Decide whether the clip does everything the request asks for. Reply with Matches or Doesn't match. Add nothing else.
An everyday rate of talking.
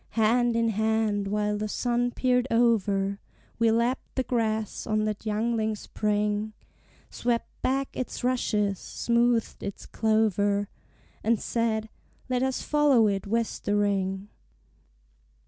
Doesn't match